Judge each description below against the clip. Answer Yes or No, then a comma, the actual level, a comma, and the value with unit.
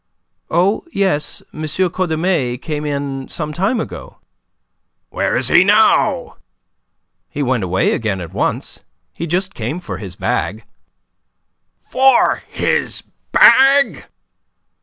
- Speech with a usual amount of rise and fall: No, wide, 6.9 semitones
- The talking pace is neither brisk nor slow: No, slow, 115 wpm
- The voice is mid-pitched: Yes, medium, 155 Hz